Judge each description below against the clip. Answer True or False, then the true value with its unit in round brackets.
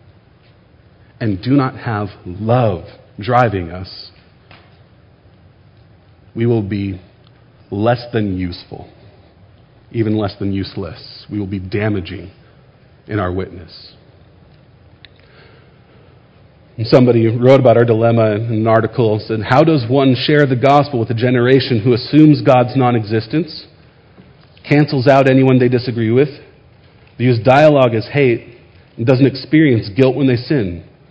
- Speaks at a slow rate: True (125 wpm)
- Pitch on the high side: False (120 Hz)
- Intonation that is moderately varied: True (4.2 semitones)